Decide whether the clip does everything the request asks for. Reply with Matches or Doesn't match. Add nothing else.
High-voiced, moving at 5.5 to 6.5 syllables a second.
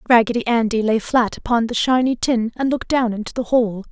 Matches